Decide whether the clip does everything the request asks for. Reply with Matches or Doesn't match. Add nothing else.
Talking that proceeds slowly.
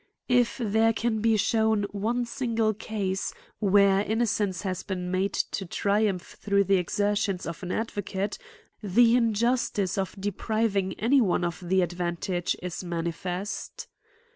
Matches